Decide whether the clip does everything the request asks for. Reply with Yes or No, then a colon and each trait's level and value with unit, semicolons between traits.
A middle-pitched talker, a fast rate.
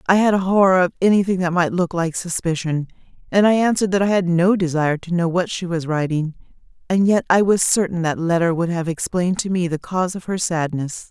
Yes: medium, 175 Hz; fast, 225 wpm